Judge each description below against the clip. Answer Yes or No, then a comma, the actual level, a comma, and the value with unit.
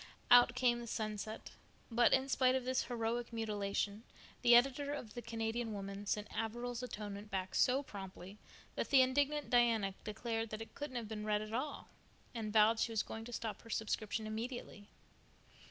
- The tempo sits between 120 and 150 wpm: No, average, 175 wpm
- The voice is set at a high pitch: Yes, high, 225 Hz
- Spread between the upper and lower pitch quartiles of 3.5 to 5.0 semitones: No, narrow, 2.5 semitones